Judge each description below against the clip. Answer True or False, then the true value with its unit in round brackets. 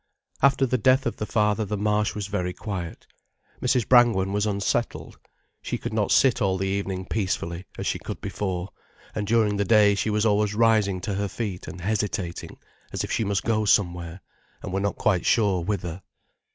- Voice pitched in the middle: False (105 Hz)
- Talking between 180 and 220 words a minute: True (190 wpm)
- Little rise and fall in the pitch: True (2.3 semitones)